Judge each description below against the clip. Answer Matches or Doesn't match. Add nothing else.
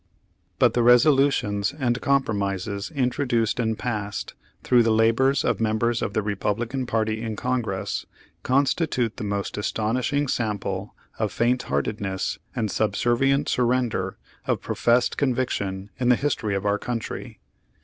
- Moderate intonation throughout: Matches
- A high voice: Doesn't match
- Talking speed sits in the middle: Doesn't match